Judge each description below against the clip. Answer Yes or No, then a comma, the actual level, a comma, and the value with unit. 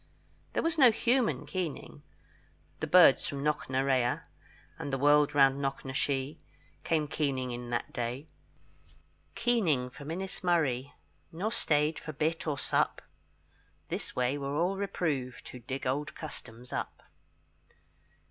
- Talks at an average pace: No, slow, 125 wpm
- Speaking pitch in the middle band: Yes, medium, 145 Hz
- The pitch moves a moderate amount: Yes, average, 3.9 semitones